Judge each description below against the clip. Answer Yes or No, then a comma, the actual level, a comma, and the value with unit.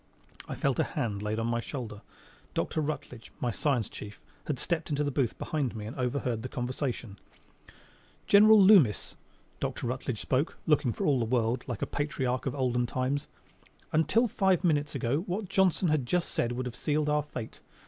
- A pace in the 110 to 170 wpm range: No, average, 180 wpm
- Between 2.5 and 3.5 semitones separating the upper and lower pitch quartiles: No, average, 4.2 semitones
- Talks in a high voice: No, low, 130 Hz